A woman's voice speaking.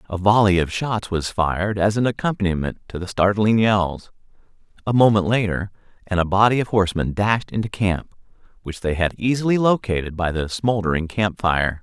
No: male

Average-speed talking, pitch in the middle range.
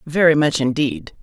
Yes: average, 145 wpm; medium, 145 Hz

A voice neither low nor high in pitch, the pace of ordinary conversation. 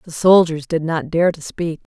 No: medium, 165 Hz; fast, 215 wpm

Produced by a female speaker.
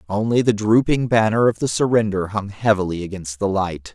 No: male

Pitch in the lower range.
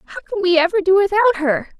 No: very high, 370 Hz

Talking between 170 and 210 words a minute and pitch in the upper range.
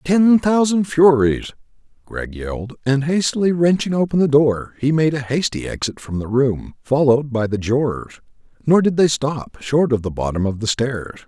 No: average, 175 wpm; medium, 140 Hz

